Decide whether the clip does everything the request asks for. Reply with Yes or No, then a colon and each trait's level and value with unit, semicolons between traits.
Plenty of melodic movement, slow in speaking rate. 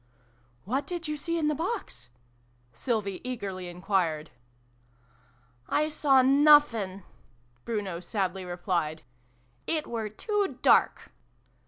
Yes: wide, 8.9 semitones; slow, 115 wpm